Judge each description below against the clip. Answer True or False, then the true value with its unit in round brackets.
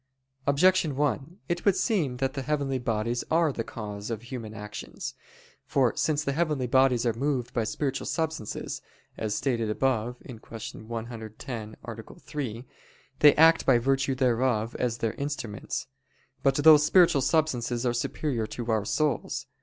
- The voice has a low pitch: True (130 Hz)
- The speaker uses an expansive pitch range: False (4.2 semitones)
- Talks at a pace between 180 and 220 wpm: False (150 wpm)